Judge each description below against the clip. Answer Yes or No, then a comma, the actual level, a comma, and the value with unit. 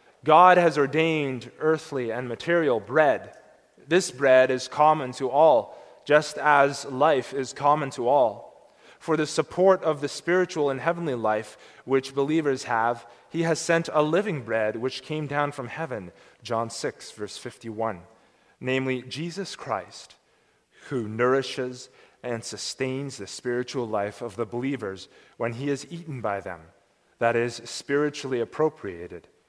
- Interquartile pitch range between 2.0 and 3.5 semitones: No, average, 4.4 semitones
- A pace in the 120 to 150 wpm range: Yes, average, 140 wpm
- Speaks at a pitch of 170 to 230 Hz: No, low, 135 Hz